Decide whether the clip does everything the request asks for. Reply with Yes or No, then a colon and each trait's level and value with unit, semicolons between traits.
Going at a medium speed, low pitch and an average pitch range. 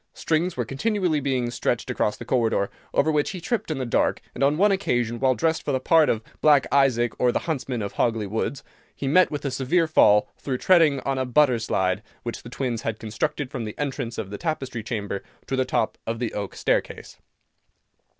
No: fast, 210 wpm; low, 130 Hz; average, 4.7 semitones